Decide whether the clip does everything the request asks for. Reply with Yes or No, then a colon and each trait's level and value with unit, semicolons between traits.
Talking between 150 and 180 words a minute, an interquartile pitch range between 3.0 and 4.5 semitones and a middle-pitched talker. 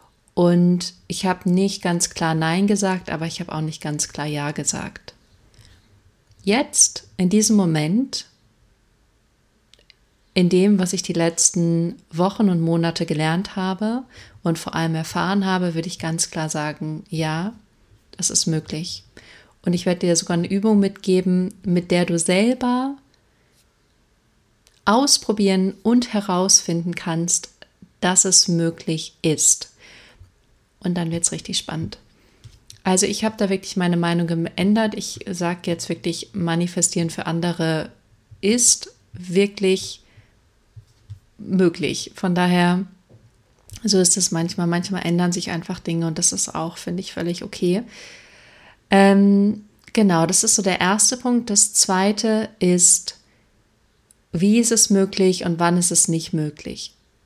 No: average, 135 wpm; average, 3.4 semitones; medium, 175 Hz